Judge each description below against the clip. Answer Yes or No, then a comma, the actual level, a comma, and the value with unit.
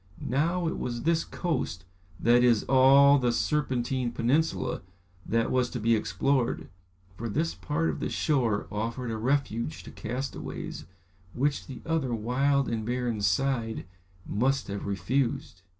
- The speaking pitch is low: Yes, low, 125 Hz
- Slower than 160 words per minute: Yes, average, 140 wpm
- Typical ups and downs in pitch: Yes, average, 3.4 semitones